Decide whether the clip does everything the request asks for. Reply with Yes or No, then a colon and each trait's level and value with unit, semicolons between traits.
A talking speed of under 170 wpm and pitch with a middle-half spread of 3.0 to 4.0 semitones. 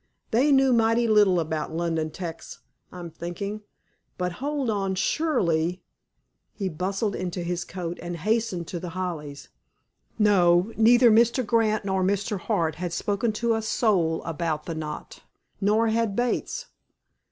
No: average, 140 wpm; average, 4.7 semitones